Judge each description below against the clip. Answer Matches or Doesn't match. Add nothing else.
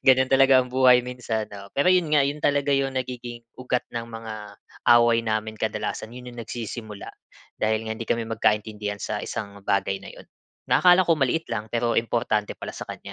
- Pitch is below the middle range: Matches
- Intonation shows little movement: Doesn't match